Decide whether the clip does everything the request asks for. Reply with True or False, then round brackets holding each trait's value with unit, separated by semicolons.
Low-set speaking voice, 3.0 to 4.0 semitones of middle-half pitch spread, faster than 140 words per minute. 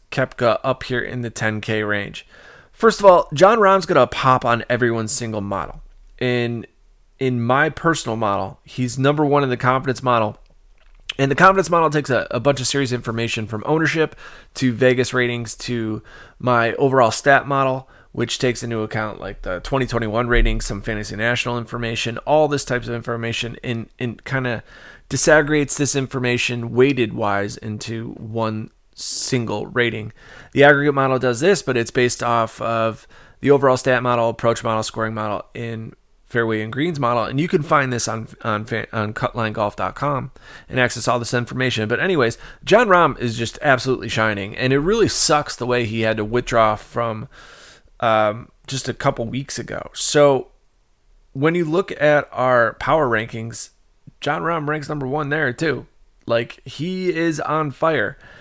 True (125 Hz; 3.5 semitones; 170 wpm)